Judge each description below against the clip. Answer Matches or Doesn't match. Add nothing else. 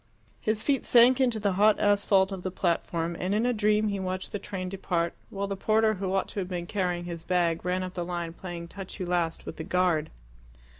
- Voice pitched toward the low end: Doesn't match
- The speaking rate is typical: Doesn't match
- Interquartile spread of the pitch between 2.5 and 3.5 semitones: Matches